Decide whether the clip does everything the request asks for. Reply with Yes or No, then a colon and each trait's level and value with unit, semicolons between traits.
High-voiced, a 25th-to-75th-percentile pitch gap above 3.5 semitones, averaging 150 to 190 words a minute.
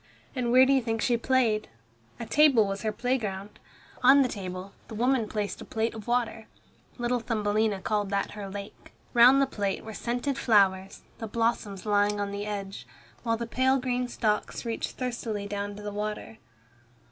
No: high, 220 Hz; average, 3.1 semitones; average, 180 wpm